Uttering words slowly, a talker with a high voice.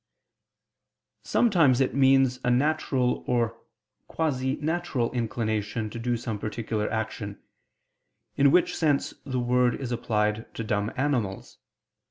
No: slow, 120 wpm; low, 125 Hz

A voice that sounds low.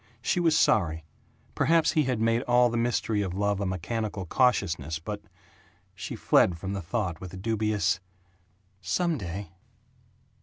Yes: low, 105 Hz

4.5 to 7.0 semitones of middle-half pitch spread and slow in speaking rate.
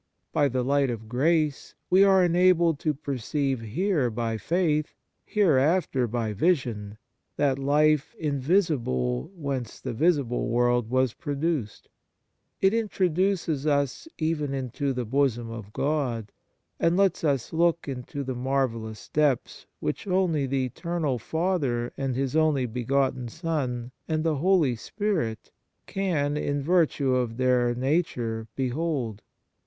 Yes: average, 4.9 semitones; slow, 125 wpm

